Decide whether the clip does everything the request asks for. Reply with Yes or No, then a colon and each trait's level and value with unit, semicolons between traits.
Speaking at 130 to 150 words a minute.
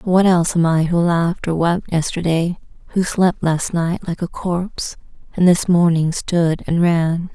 No: average, 180 wpm